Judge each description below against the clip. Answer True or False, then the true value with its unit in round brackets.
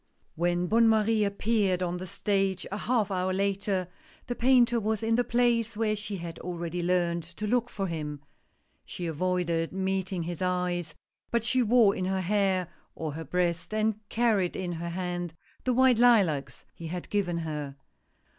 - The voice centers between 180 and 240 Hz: True (190 Hz)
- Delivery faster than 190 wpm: False (175 wpm)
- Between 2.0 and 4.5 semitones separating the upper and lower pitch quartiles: True (3.8 semitones)